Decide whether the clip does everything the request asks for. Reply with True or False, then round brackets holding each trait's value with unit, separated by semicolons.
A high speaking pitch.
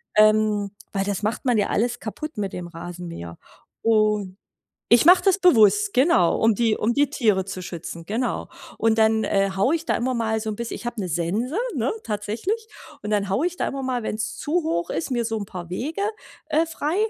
True (220 Hz)